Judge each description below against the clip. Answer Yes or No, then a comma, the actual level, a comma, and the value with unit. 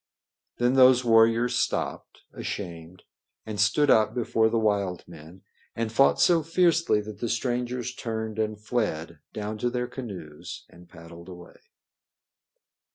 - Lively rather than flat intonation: No, average, 4.7 semitones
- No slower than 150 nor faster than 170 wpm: No, slow, 135 wpm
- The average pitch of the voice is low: Yes, low, 110 Hz